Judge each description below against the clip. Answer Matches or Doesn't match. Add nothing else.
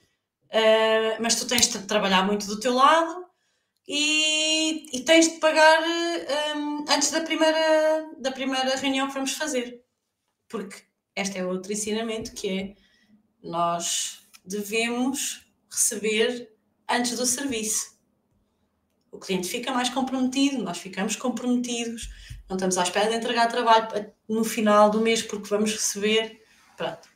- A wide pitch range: Doesn't match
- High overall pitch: Matches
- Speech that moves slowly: Doesn't match